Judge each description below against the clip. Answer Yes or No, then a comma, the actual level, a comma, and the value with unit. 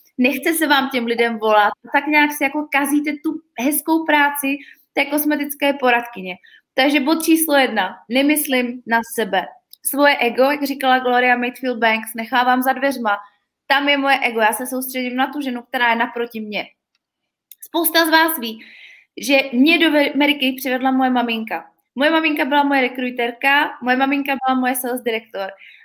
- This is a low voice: No, very high, 265 Hz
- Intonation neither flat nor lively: Yes, average, 3.2 semitones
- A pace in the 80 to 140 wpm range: No, average, 160 wpm